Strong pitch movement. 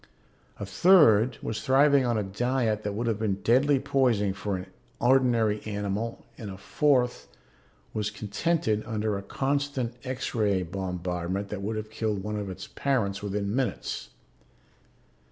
No: average, 4.0 semitones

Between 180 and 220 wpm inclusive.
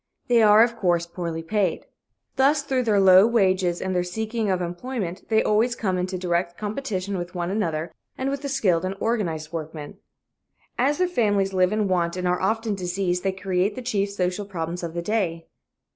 Yes: average, 190 wpm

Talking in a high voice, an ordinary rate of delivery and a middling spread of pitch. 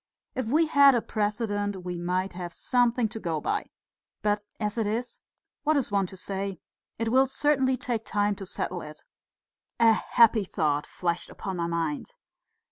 Yes: high, 205 Hz; average, 170 wpm; average, 4.9 semitones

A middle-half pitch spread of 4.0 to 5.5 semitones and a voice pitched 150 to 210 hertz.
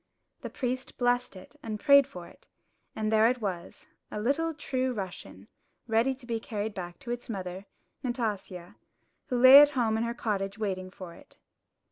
No: average, 4.5 semitones; high, 225 Hz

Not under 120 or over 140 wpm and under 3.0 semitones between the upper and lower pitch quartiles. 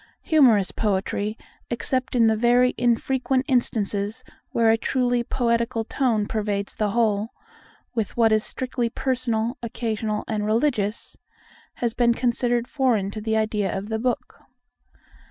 Yes: slow, 135 wpm; narrow, 2.4 semitones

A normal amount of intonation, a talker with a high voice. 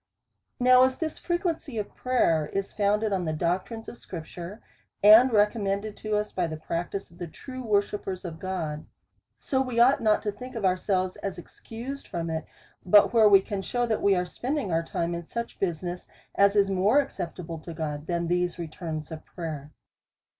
Yes: average, 4.7 semitones; high, 195 Hz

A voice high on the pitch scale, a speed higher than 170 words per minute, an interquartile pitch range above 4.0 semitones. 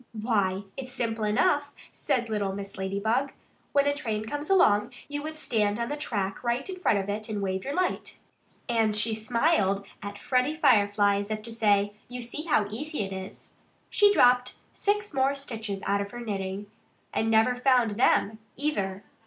Yes: high, 225 Hz; average, 185 wpm; average, 4.8 semitones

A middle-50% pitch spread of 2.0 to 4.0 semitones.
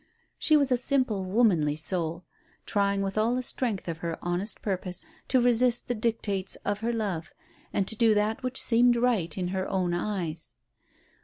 No: average, 4.6 semitones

